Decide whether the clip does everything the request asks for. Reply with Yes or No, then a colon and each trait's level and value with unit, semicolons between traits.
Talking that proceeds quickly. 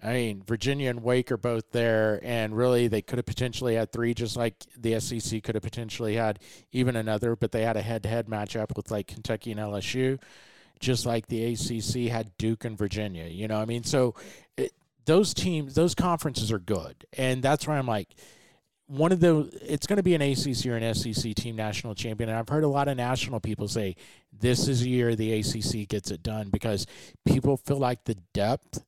Yes: fast, 210 wpm